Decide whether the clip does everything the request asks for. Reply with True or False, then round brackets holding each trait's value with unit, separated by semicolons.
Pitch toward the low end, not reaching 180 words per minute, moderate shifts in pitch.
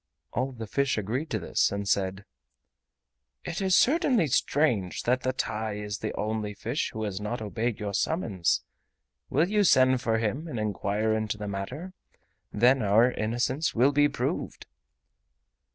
True (115 Hz; 155 wpm; 4.6 semitones)